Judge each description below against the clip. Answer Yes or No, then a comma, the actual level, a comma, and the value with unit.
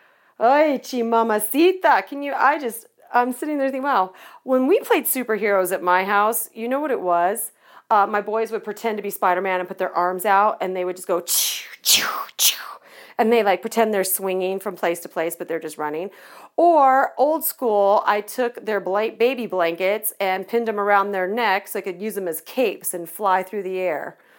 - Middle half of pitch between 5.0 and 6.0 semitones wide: No, average, 4.2 semitones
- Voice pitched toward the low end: No, high, 205 Hz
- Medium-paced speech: No, fast, 210 wpm